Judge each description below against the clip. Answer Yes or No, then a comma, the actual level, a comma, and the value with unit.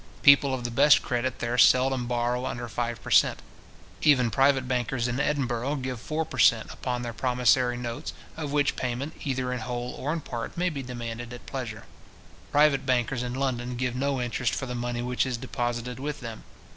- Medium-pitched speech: No, low, 125 Hz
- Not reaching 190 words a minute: No, average, 195 wpm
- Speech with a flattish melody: Yes, narrow, 1.9 semitones